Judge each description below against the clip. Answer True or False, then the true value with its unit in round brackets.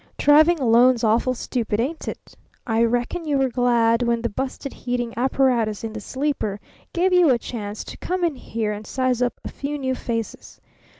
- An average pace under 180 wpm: False (185 wpm)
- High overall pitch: True (245 Hz)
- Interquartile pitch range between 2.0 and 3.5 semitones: True (3.1 semitones)